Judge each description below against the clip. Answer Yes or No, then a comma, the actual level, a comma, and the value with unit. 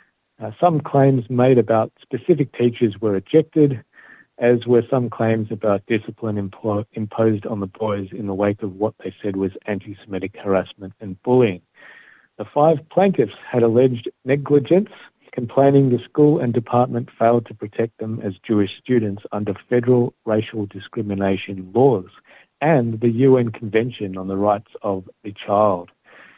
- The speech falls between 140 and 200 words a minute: Yes, fast, 150 wpm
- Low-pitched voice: Yes, low, 115 Hz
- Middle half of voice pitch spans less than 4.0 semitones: Yes, average, 3.5 semitones